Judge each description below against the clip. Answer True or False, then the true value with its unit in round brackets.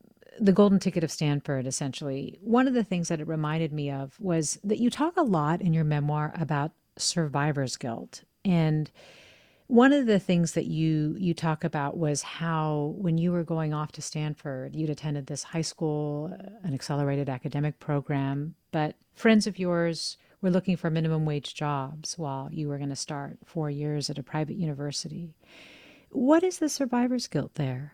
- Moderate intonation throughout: True (3.5 semitones)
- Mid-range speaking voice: True (155 Hz)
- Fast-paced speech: False (175 wpm)